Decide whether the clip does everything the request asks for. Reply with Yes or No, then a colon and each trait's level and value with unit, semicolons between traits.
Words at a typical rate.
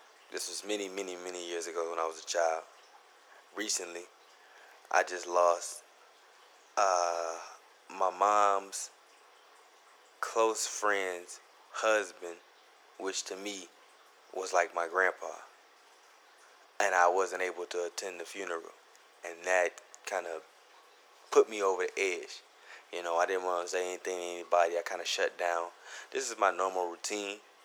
Yes: average, 145 wpm